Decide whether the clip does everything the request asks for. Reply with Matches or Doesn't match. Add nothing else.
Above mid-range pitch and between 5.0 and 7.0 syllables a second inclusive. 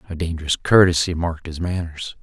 Doesn't match